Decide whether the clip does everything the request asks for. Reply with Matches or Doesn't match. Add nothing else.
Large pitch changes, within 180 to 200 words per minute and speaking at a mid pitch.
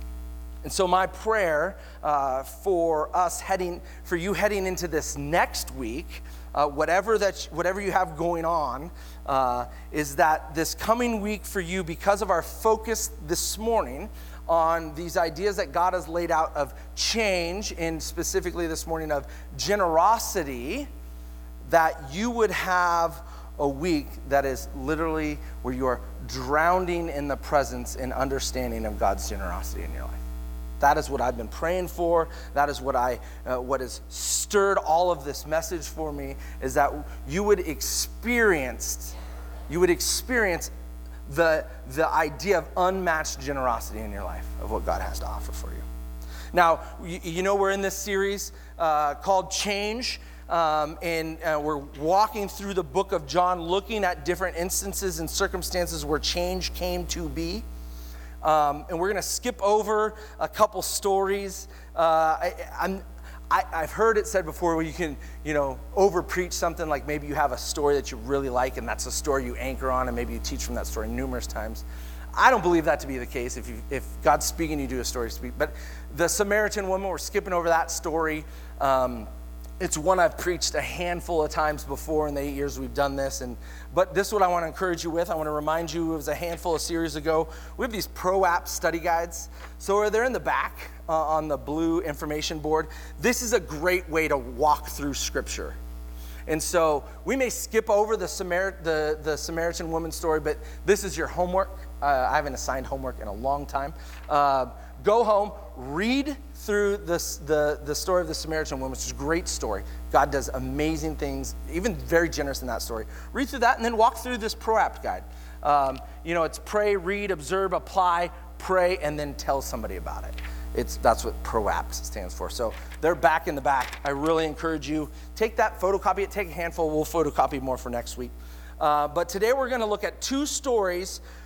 Matches